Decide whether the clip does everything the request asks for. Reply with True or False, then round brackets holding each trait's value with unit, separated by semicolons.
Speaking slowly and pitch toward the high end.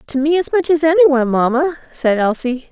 False (200 wpm; 285 Hz)